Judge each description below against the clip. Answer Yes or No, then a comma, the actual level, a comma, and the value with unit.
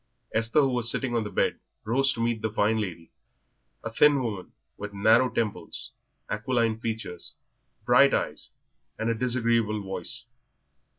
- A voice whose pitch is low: Yes, low, 115 Hz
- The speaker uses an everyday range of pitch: No, narrow, 2.1 semitones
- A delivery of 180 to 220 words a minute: No, average, 150 wpm